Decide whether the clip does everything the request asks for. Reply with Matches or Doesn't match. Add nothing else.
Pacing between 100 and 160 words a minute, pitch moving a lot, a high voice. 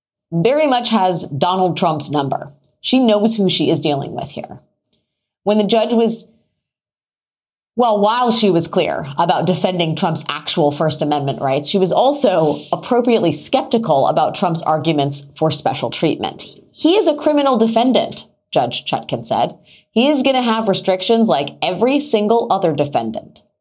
Matches